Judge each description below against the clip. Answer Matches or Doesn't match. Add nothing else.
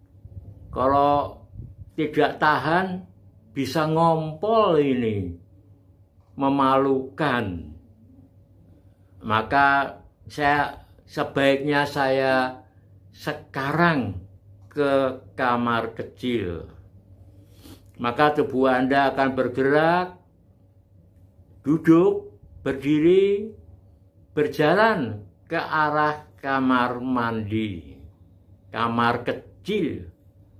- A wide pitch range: Matches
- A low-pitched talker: Matches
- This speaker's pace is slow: Matches